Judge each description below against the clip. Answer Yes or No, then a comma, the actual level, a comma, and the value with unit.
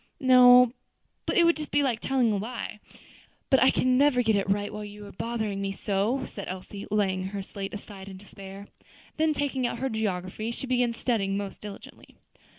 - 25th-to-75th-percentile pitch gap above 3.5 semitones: Yes, average, 4.1 semitones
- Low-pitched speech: No, high, 215 Hz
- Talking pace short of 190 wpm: No, average, 195 wpm